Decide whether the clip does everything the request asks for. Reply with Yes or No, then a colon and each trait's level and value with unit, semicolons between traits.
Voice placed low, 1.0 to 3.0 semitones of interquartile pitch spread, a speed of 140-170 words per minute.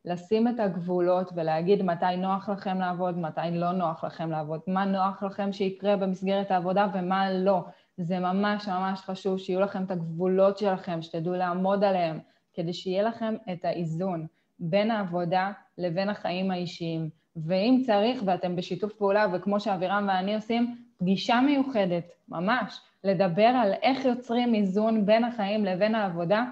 No: high, 190 Hz; narrow, 2.5 semitones; average, 145 wpm